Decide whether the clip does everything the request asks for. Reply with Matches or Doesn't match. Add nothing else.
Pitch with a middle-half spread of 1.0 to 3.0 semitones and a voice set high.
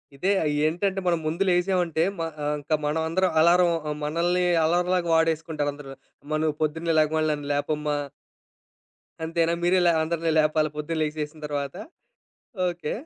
Doesn't match